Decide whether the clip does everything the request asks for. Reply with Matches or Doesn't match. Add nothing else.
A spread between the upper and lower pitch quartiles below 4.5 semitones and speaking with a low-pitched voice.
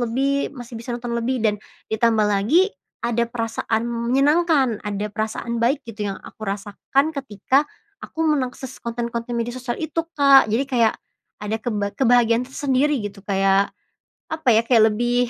Doesn't match